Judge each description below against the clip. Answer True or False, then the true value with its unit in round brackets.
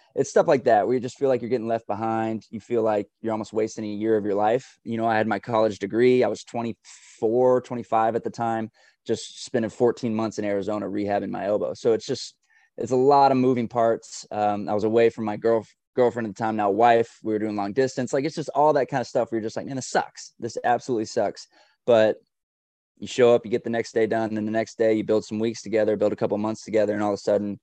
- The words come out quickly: True (265 wpm)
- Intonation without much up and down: True (2.3 semitones)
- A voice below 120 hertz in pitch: True (110 Hz)